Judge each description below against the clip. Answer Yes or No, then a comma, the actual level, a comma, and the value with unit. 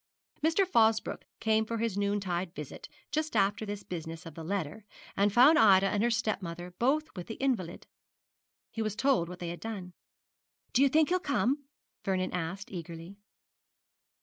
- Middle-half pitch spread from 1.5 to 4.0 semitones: No, average, 4.8 semitones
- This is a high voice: Yes, high, 205 Hz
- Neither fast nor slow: Yes, average, 165 wpm